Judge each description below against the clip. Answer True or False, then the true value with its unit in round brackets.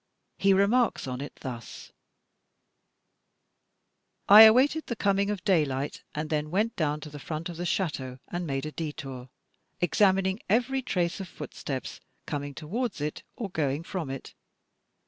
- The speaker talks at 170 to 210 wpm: False (145 wpm)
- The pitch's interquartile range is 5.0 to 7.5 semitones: True (5.4 semitones)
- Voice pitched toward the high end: False (170 Hz)